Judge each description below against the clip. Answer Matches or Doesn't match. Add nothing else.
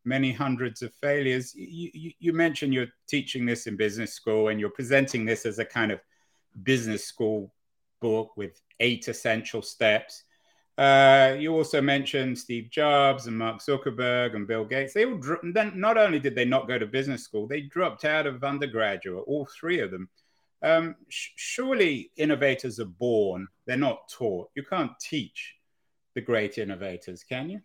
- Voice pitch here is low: Matches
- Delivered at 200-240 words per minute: Doesn't match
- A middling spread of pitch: Matches